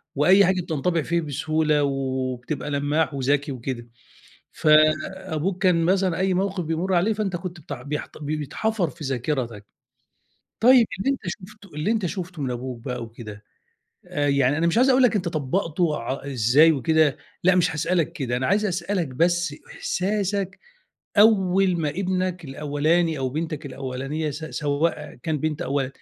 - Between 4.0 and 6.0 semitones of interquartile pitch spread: Yes, average, 4.7 semitones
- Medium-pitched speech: Yes, medium, 160 Hz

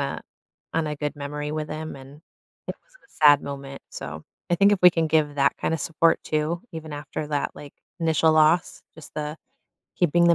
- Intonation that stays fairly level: Yes, narrow, 2.0 semitones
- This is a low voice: No, medium, 155 Hz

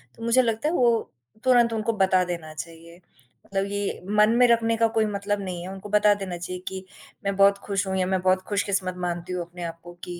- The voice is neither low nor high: No, high, 195 Hz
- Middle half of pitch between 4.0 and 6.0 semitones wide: No, average, 3.3 semitones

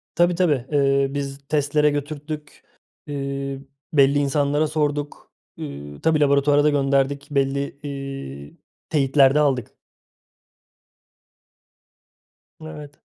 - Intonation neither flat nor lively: No, narrow, 1.4 semitones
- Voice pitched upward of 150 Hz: No, medium, 140 Hz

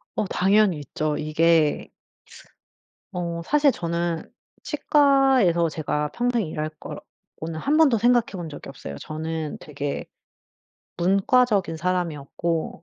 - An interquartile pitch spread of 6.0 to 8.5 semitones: Yes, wide, 6.4 semitones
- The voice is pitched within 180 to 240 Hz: No, medium, 170 Hz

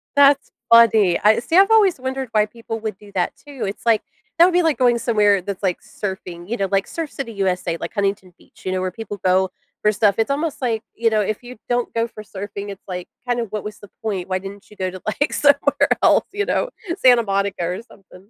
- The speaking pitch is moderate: No, high, 215 Hz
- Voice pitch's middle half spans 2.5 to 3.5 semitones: No, average, 4.0 semitones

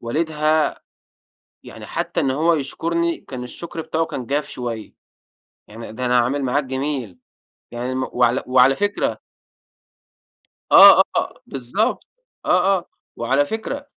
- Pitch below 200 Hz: Yes, low, 135 Hz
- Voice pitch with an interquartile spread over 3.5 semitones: Yes, average, 4.7 semitones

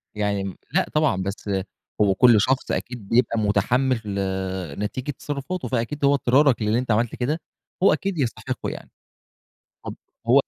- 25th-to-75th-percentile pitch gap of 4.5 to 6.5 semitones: Yes, average, 4.8 semitones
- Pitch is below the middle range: Yes, low, 120 Hz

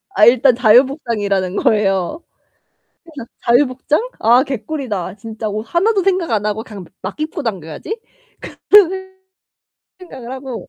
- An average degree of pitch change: No, wide, 6.6 semitones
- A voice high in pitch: Yes, high, 245 Hz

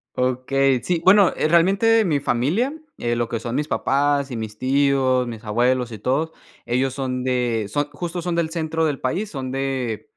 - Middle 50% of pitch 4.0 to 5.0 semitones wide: Yes, average, 4.4 semitones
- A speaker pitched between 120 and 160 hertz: Yes, low, 135 Hz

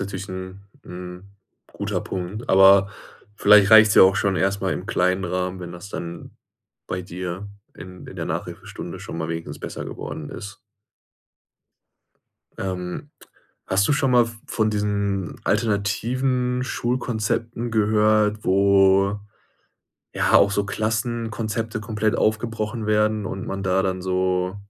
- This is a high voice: No, low, 100 Hz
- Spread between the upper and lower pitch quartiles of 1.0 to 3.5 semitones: Yes, average, 2.7 semitones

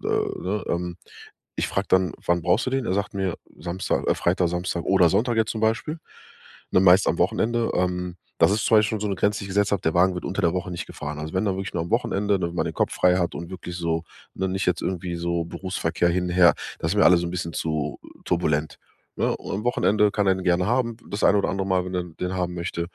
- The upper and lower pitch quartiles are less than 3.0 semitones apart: Yes, narrow, 2.5 semitones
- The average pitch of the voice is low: Yes, very low, 90 Hz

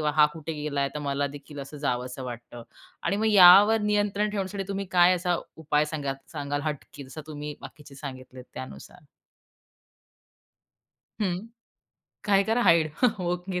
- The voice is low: No, medium, 155 Hz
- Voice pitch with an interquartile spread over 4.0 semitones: Yes, average, 5.1 semitones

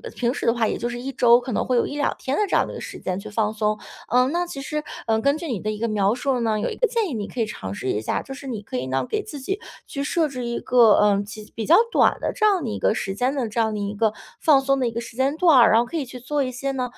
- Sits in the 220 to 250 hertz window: Yes, high, 245 Hz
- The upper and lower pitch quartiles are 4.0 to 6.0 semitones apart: Yes, average, 4.5 semitones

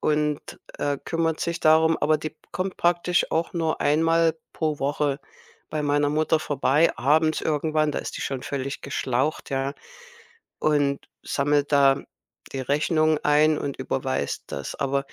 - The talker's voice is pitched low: No, medium, 150 Hz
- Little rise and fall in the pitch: Yes, narrow, 2.2 semitones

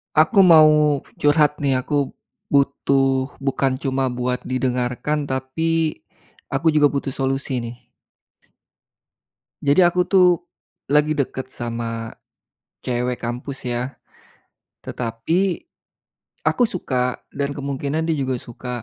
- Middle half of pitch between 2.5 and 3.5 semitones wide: Yes, average, 3.0 semitones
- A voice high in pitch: No, low, 135 Hz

